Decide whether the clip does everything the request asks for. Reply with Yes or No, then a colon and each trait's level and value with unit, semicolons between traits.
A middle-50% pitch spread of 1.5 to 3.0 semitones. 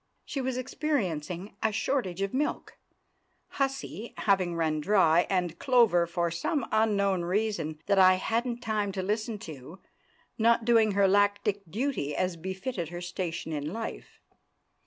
No: average, 4.5 semitones